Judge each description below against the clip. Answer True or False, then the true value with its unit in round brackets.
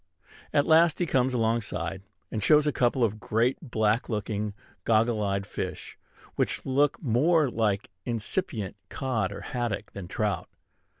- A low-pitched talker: True (115 Hz)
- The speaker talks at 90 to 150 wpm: True (140 wpm)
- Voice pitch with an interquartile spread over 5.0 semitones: False (4.0 semitones)